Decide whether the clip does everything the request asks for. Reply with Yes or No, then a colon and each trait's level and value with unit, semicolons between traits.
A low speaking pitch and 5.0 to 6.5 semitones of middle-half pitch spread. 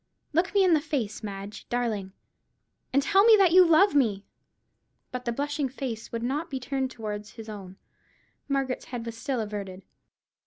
No: very high, 250 Hz; wide, 5.4 semitones